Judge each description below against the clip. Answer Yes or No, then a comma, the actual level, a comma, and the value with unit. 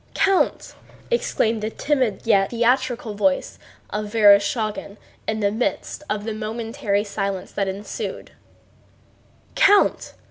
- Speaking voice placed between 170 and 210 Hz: No, high, 220 Hz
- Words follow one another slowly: Yes, slow, 110 wpm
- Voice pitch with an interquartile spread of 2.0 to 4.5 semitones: Yes, average, 2.9 semitones